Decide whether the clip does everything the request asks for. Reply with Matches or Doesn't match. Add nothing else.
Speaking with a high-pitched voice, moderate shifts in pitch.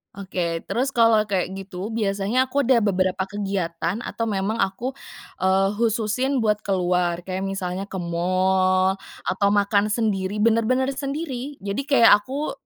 Matches